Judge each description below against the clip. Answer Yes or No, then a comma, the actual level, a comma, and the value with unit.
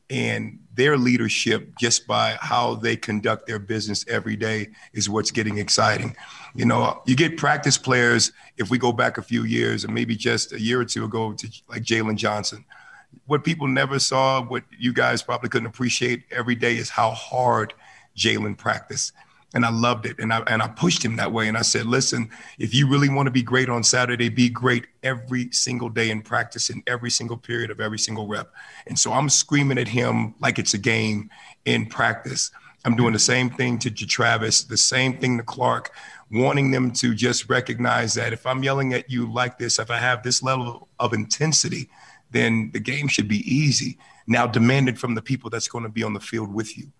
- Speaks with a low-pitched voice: Yes, low, 120 Hz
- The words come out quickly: Yes, fast, 210 wpm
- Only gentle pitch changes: Yes, narrow, 2.0 semitones